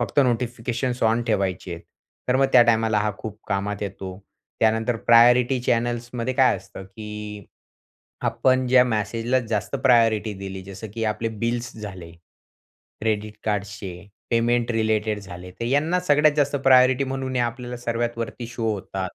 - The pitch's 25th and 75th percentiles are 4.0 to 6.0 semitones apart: No, average, 2.9 semitones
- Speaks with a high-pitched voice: No, low, 115 Hz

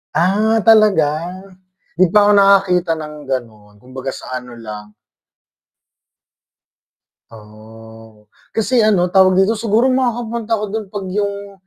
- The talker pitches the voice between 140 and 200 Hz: Yes, high, 190 Hz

